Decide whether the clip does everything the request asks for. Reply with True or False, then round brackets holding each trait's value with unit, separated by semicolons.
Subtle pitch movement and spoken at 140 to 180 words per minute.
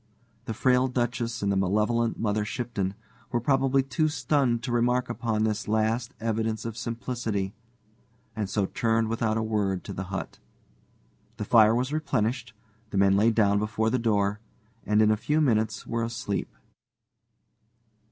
True (2.3 semitones; 155 wpm)